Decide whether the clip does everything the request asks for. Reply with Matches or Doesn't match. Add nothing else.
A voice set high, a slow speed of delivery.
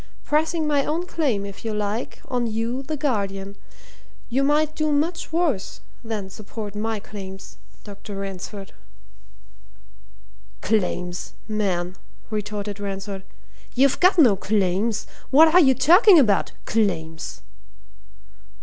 Matches